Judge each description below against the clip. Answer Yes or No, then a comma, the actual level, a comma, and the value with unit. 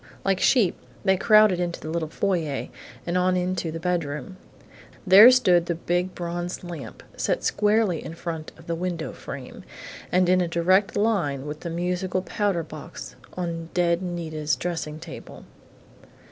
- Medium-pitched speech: Yes, medium, 175 Hz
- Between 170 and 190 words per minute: No, average, 155 wpm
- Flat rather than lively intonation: Yes, narrow, 2.0 semitones